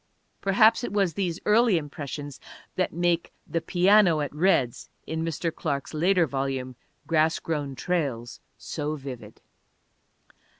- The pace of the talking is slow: Yes, slow, 125 wpm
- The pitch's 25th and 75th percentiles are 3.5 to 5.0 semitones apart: Yes, average, 4.2 semitones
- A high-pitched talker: No, medium, 160 Hz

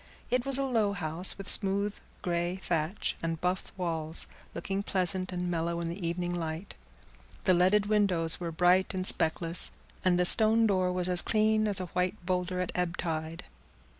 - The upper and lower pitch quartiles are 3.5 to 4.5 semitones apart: No, average, 2.7 semitones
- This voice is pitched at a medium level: Yes, medium, 180 Hz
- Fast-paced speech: No, average, 175 wpm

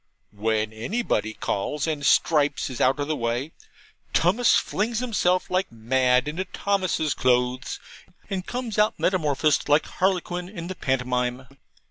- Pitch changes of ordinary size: No, wide, 6.8 semitones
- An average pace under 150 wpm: Yes, slow, 135 wpm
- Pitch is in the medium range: Yes, medium, 150 Hz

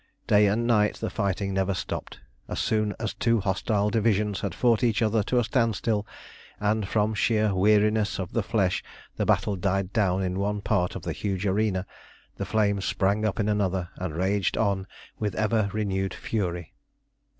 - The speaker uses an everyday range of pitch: No, narrow, 2.0 semitones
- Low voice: Yes, low, 105 Hz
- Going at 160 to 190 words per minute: Yes, average, 175 wpm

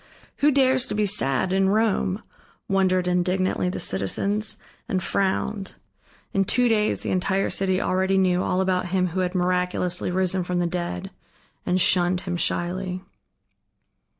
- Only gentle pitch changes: Yes, narrow, 1.4 semitones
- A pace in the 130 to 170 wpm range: Yes, average, 150 wpm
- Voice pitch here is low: No, medium, 185 Hz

